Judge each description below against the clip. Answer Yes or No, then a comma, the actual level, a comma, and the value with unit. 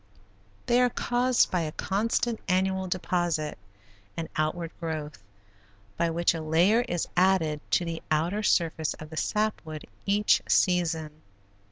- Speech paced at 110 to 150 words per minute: Yes, average, 140 wpm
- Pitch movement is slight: No, average, 3.8 semitones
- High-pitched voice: No, medium, 175 Hz